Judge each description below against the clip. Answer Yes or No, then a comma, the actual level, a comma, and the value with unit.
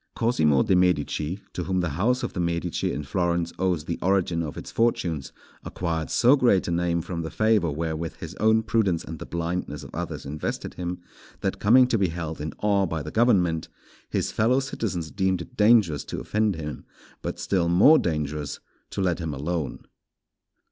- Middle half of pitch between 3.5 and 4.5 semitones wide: Yes, average, 3.9 semitones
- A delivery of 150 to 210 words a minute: Yes, average, 185 wpm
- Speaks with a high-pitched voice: No, very low, 85 Hz